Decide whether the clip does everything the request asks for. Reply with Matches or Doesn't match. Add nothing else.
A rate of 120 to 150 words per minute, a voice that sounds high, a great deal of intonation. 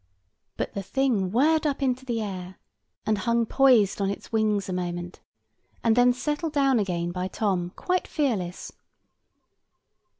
Matches